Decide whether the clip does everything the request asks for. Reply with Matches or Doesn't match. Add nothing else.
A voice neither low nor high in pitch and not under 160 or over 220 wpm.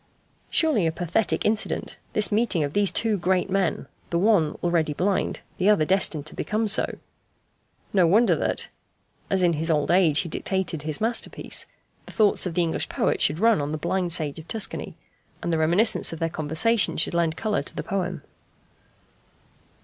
Matches